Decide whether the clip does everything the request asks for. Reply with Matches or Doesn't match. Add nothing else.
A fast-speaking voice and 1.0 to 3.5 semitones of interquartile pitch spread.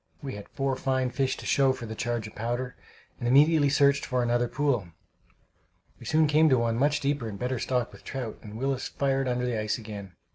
Matches